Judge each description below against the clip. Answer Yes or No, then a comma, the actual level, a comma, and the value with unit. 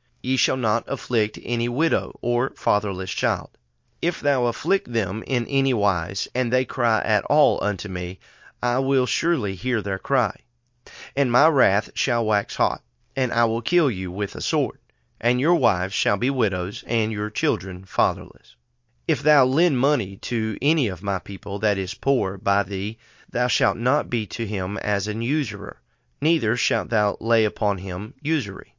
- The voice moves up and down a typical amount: Yes, average, 4.4 semitones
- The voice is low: Yes, low, 115 Hz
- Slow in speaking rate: No, average, 175 wpm